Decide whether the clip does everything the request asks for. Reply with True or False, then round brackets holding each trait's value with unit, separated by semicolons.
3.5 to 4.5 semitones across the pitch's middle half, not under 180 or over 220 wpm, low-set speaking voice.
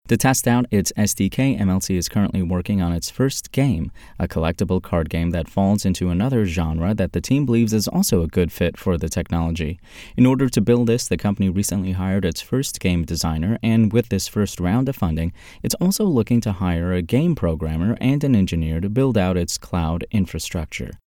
False (5.2 semitones; 200 wpm; 95 Hz)